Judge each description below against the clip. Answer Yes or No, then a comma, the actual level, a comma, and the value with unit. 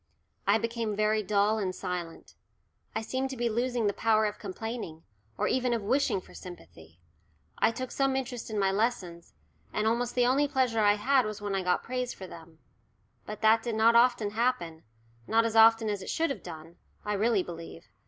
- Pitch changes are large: No, average, 3.8 semitones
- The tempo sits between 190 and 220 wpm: Yes, average, 195 wpm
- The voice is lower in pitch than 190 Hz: No, high, 220 Hz